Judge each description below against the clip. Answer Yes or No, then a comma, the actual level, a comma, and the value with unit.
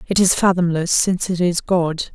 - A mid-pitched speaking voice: Yes, medium, 175 Hz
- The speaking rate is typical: Yes, average, 195 wpm